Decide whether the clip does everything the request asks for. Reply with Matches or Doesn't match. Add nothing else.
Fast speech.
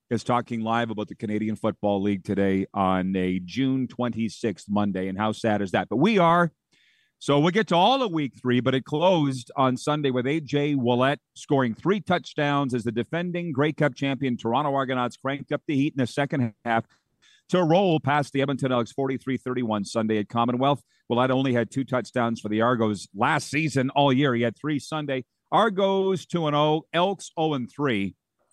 Doesn't match